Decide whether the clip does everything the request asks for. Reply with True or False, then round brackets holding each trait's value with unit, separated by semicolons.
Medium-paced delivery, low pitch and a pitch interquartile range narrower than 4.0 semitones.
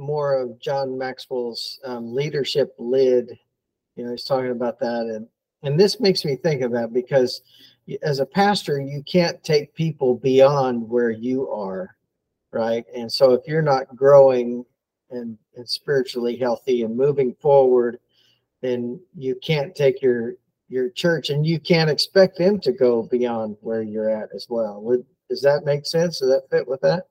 False (170 wpm; 130 Hz; 4.6 semitones)